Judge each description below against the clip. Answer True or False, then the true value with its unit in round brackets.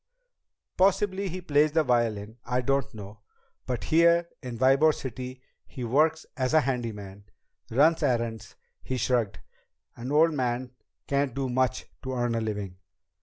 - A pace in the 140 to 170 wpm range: True (145 wpm)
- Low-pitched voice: True (130 Hz)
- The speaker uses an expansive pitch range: False (4.3 semitones)